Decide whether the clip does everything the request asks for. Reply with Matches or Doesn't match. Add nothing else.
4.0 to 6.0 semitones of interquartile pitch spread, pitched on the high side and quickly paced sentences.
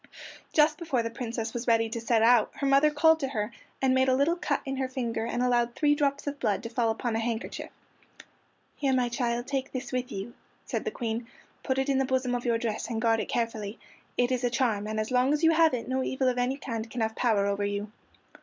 Doesn't match